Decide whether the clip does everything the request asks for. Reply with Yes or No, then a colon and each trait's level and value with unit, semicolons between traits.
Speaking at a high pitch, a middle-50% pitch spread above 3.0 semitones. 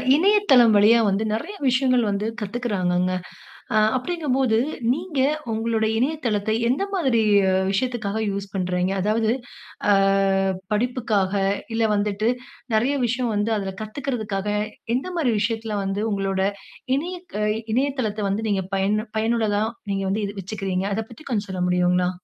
Yes: high, 220 Hz; average, 3.9 semitones